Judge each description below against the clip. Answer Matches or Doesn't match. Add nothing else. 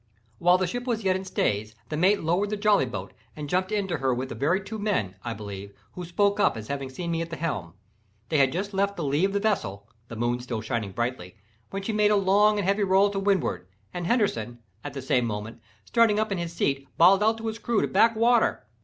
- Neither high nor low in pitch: Matches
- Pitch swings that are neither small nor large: Doesn't match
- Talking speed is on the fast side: Matches